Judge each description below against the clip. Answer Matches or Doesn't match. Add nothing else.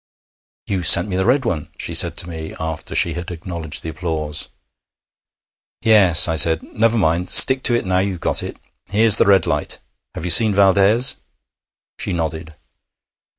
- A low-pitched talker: Matches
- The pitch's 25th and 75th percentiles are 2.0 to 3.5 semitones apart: Doesn't match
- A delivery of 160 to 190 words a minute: Matches